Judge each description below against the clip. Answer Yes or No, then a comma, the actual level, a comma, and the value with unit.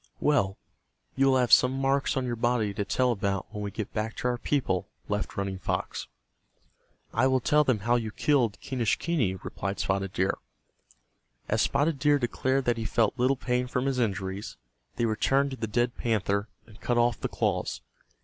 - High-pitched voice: No, low, 120 Hz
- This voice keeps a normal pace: Yes, average, 185 wpm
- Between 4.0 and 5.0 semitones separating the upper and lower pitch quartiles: Yes, average, 4.3 semitones